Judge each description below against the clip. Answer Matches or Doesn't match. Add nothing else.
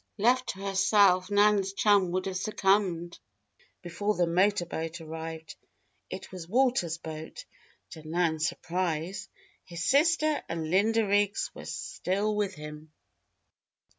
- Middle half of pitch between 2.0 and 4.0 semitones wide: Matches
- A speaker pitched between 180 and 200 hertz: Matches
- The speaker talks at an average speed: Doesn't match